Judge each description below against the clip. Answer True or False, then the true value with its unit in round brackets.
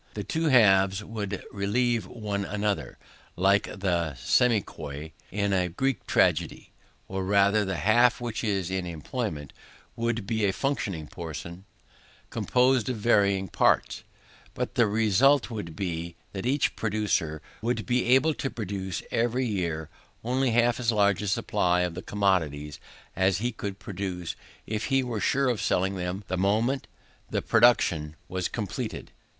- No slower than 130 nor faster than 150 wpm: True (145 wpm)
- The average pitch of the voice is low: True (100 Hz)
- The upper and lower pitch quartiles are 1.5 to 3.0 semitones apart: False (4.3 semitones)